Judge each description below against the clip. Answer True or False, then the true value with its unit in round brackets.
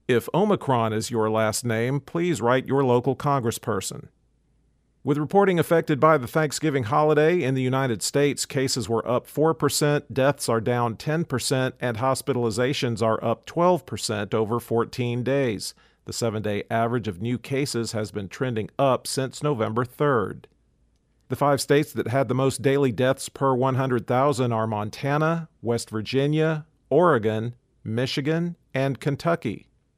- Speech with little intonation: False (4.0 semitones)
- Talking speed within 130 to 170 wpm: True (140 wpm)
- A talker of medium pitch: False (130 Hz)